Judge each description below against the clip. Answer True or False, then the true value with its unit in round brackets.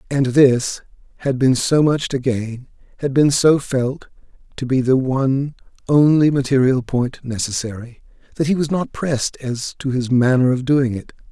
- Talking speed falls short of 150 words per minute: False (170 wpm)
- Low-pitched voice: True (130 Hz)